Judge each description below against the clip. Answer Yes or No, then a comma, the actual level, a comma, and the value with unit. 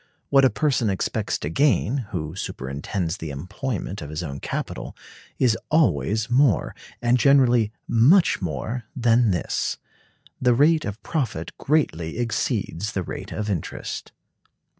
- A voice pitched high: No, low, 110 Hz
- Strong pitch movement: Yes, wide, 6.8 semitones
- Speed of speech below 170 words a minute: Yes, slow, 135 wpm